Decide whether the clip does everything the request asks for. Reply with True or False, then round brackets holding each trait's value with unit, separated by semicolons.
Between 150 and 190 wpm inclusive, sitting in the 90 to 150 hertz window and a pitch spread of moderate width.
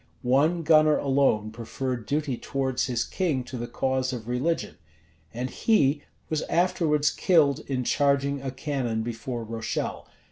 False (140 wpm; 135 Hz; 3.5 semitones)